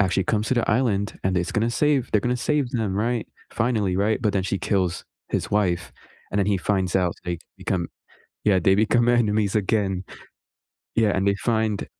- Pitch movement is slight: No, average, 3.1 semitones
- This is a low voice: Yes, low, 105 Hz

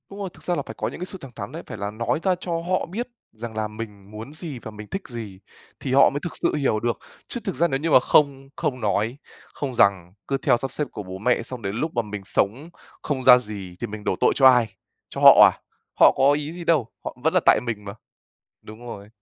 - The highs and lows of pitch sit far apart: Yes, wide, 5.9 semitones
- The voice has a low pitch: Yes, low, 125 Hz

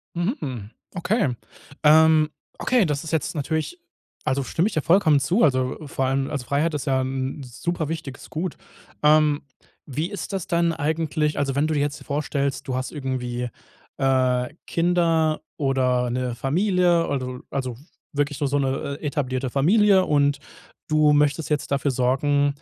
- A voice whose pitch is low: No, medium, 145 Hz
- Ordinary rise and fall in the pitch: Yes, average, 3.2 semitones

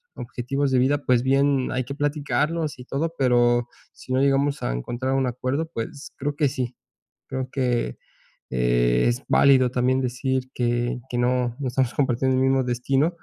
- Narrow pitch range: Yes, narrow, 2.1 semitones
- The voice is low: Yes, low, 130 Hz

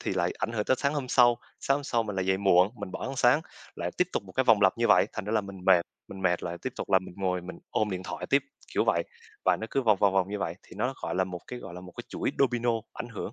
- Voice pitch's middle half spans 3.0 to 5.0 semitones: Yes, average, 4.6 semitones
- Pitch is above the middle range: No, low, 105 Hz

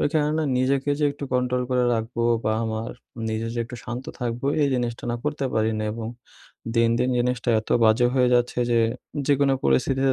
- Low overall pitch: Yes, low, 125 Hz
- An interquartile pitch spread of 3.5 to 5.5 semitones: No, average, 2.7 semitones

